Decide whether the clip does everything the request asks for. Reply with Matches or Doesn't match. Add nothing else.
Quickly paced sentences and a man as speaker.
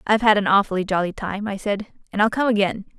Doesn't match